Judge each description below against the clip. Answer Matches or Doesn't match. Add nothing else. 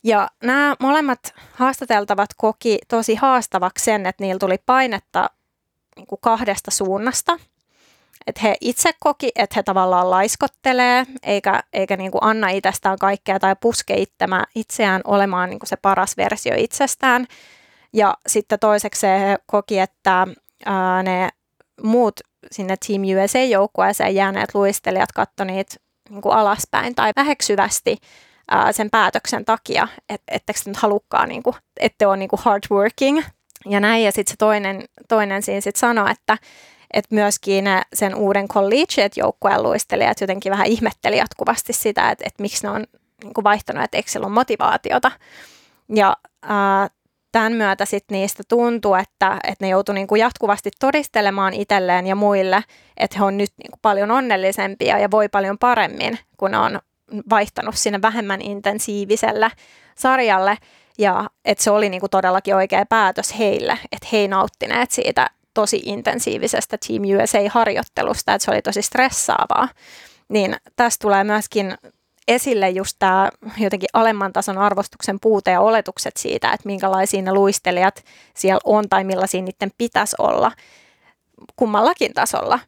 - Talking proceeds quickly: Doesn't match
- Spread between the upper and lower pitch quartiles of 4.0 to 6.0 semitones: Doesn't match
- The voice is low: Doesn't match